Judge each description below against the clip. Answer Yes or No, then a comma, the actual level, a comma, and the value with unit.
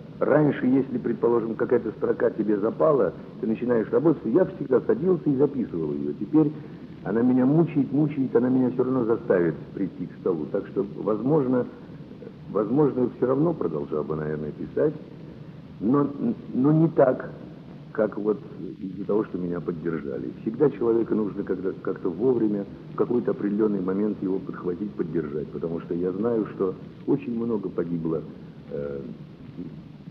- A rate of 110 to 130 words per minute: No, average, 145 wpm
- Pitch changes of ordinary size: No, wide, 8.2 semitones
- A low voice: Yes, low, 110 Hz